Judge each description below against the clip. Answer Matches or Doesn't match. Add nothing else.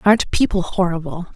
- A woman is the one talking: Matches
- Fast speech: Doesn't match